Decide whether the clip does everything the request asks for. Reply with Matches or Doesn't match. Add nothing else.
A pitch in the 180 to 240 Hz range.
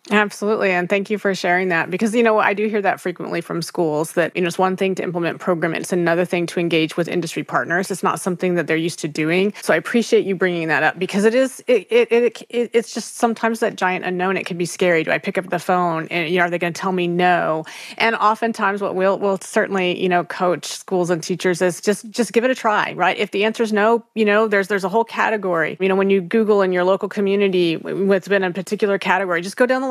Matches